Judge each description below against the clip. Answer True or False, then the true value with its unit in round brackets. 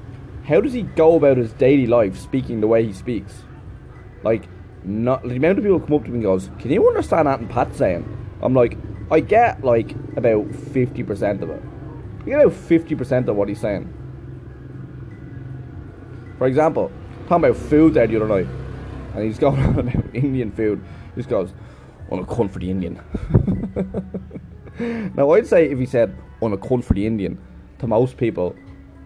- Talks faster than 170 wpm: True (190 wpm)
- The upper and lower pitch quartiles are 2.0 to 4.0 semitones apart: False (4.6 semitones)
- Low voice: True (120 Hz)